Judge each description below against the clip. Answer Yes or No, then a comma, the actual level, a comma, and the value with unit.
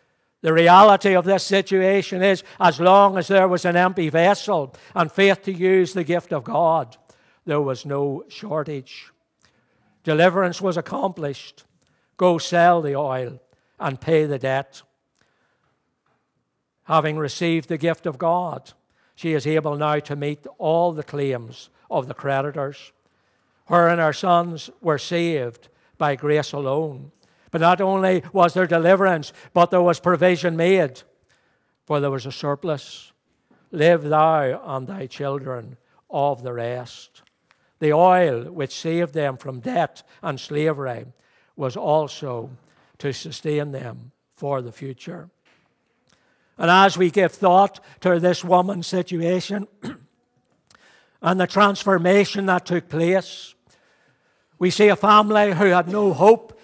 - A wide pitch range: No, average, 4.2 semitones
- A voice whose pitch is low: No, medium, 165 Hz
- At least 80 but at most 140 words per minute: Yes, slow, 135 wpm